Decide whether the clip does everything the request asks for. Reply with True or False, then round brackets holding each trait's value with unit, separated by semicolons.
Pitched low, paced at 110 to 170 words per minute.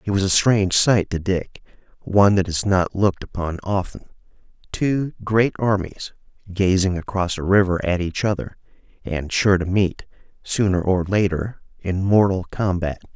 True (95 Hz; 155 wpm)